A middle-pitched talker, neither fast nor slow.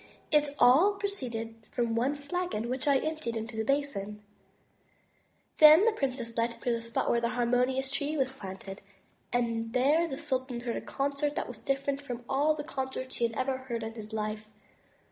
No: very high, 260 Hz; average, 185 wpm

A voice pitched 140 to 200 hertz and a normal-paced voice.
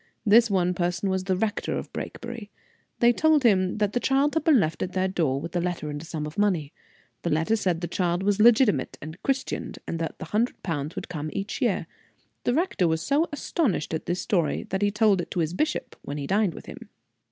No: medium, 185 Hz; fast, 230 wpm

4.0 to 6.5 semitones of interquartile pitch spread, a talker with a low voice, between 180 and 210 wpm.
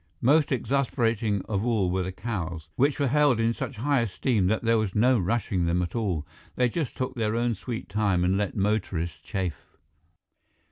Yes: average, 4.6 semitones; low, 110 Hz; average, 185 wpm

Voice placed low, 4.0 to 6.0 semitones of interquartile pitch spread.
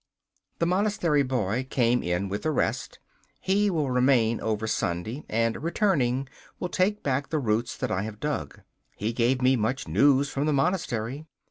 Yes: low, 130 Hz; average, 5.2 semitones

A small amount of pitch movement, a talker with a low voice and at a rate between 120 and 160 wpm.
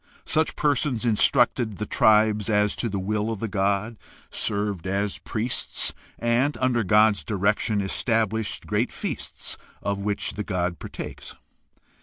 Yes: narrow, 2.2 semitones; low, 105 Hz; average, 140 wpm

